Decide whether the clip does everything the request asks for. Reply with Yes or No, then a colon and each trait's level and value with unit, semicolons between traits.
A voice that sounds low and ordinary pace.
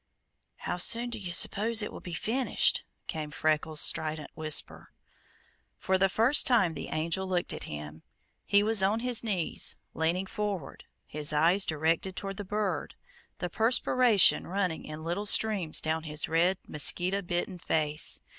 No: medium, 180 Hz; average, 155 wpm